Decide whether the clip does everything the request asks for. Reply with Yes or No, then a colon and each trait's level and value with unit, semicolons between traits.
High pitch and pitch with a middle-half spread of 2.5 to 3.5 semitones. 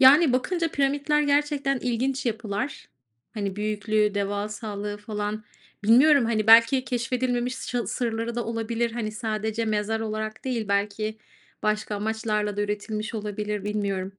Yes: high, 220 Hz; average, 2.9 semitones